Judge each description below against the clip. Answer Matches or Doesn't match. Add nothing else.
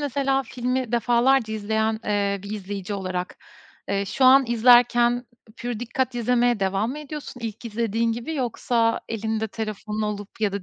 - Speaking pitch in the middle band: Doesn't match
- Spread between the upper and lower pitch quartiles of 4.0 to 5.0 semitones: Doesn't match